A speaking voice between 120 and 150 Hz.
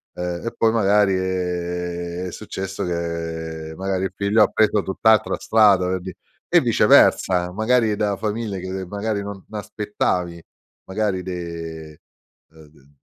No: very low, 95 Hz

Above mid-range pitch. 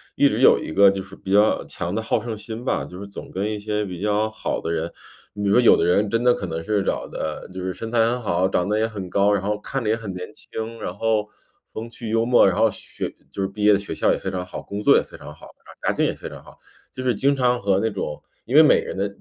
No: low, 105 Hz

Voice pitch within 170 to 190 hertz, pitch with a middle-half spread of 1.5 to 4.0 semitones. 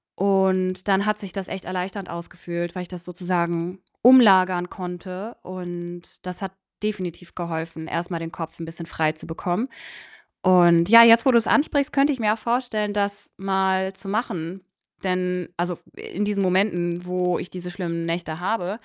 Yes: medium, 185 Hz; narrow, 2.5 semitones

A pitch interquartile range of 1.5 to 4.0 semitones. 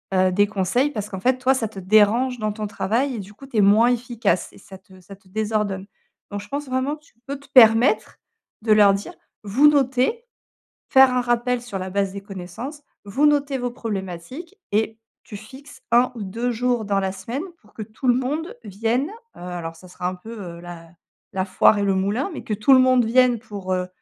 No: average, 4.6 semitones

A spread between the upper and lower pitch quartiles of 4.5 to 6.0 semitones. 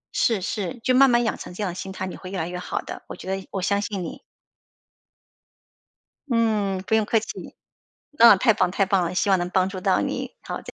No: average, 3.1 semitones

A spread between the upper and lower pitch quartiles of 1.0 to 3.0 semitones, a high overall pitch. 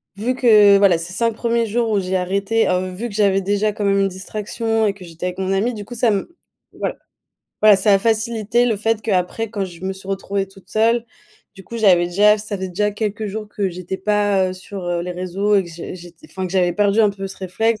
Yes: narrow, 2.6 semitones; high, 200 Hz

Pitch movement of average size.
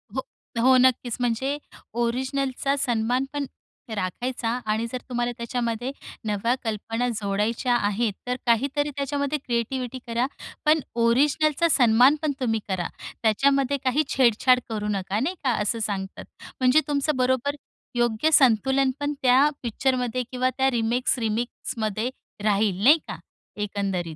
Yes: average, 3.3 semitones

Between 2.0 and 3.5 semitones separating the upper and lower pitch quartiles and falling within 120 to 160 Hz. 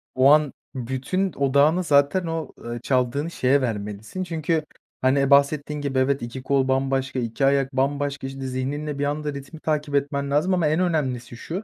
Yes: narrow, 2.4 semitones; medium, 140 Hz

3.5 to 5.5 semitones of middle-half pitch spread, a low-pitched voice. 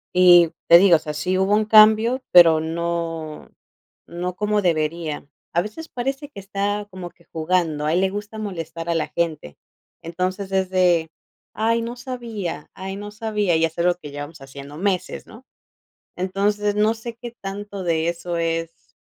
No: average, 3.9 semitones; medium, 185 Hz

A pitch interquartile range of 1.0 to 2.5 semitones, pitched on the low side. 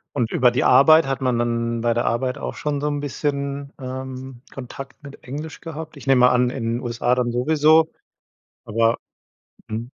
No: average, 2.9 semitones; low, 130 Hz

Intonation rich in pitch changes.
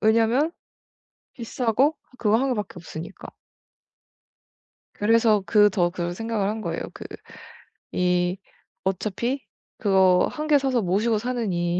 No: average, 4.2 semitones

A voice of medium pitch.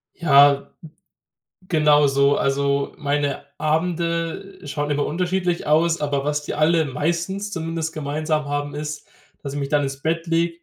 Yes: medium, 150 Hz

